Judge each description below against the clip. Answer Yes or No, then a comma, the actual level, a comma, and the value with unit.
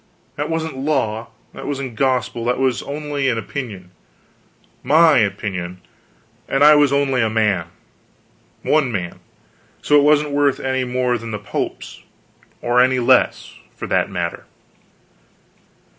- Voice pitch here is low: Yes, low, 130 Hz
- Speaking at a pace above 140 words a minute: No, slow, 135 wpm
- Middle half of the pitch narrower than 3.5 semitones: No, average, 4.3 semitones